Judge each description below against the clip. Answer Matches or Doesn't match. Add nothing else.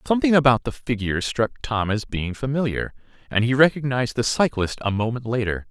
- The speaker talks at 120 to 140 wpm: Doesn't match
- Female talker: Doesn't match